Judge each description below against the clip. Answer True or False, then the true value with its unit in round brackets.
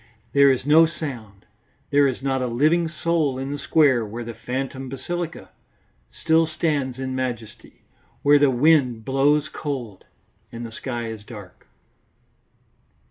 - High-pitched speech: False (135 Hz)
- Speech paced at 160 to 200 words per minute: False (140 wpm)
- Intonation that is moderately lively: True (3.9 semitones)